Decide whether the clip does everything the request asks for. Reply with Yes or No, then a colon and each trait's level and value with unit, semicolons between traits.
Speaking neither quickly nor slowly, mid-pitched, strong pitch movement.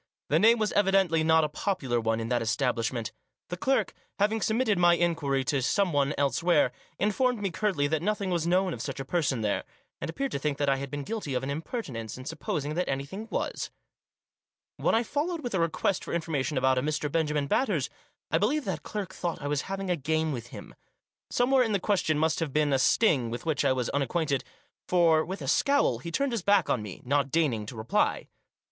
No: fast, 215 wpm; medium, 160 Hz; wide, 6.1 semitones